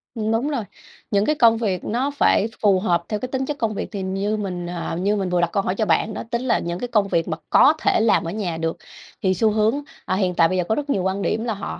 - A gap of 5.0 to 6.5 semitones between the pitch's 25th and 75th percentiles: No, average, 3.7 semitones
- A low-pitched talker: No, high, 205 Hz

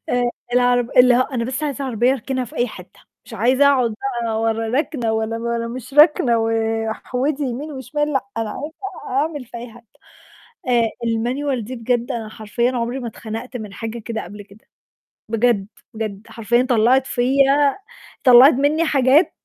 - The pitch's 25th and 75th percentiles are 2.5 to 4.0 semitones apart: Yes, average, 2.9 semitones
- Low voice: No, high, 245 Hz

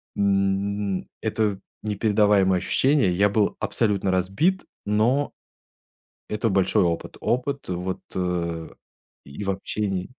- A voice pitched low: Yes, low, 100 Hz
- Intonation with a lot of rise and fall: No, narrow, 2.4 semitones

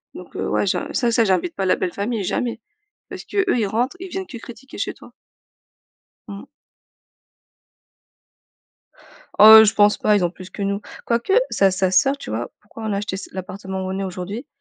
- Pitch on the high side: Yes, high, 205 Hz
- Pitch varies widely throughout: No, average, 3.7 semitones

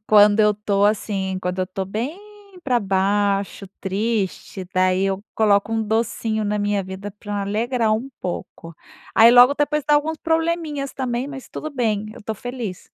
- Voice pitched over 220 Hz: No, high, 210 Hz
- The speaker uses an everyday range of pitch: Yes, average, 3.8 semitones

